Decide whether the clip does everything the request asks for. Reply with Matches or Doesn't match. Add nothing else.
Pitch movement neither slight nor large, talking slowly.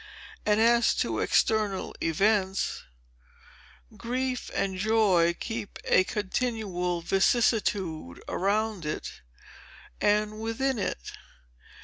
Matches